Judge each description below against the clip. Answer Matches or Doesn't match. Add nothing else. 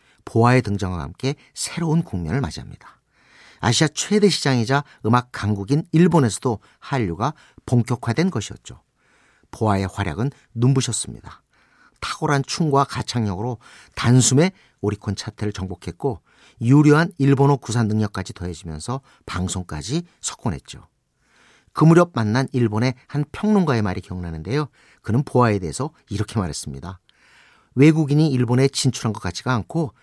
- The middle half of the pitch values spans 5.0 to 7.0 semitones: Matches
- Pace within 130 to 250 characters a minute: Doesn't match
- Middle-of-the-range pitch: Doesn't match